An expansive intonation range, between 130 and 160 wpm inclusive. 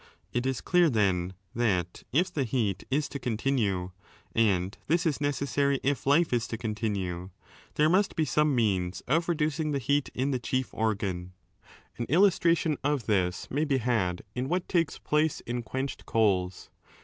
No: wide, 6.4 semitones; average, 170 wpm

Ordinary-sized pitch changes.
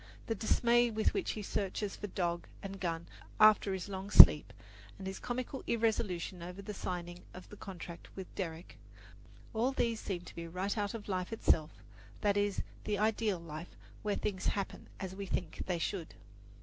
Yes: average, 3.1 semitones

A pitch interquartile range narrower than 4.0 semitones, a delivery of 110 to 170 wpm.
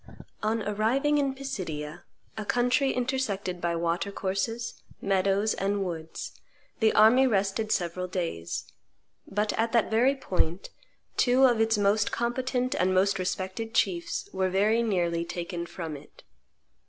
No: average, 4.6 semitones; slow, 135 wpm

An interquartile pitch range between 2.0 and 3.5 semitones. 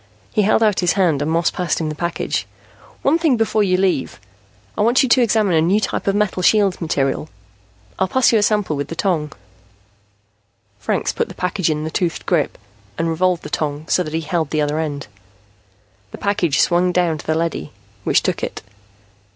No: average, 4.3 semitones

